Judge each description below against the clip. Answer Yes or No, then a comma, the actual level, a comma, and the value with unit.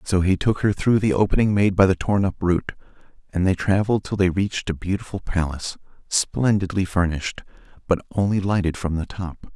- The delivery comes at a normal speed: Yes, average, 190 wpm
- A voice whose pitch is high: No, very low, 95 Hz